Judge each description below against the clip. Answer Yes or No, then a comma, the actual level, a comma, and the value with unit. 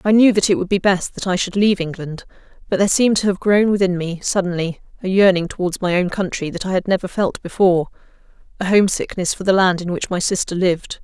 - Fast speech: Yes, fast, 235 wpm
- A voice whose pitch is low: No, high, 190 Hz